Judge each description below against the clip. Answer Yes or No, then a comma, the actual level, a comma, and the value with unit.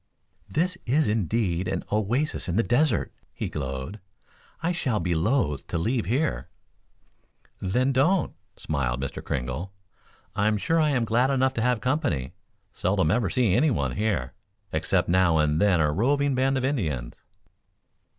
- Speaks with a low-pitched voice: Yes, low, 110 Hz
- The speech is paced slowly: No, average, 150 wpm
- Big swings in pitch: Yes, wide, 8.3 semitones